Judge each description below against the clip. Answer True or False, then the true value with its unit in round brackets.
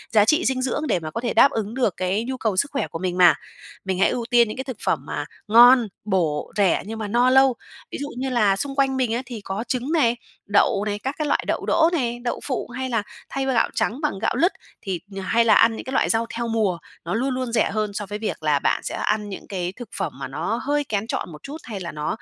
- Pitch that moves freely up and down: False (4.6 semitones)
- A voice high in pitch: True (230 Hz)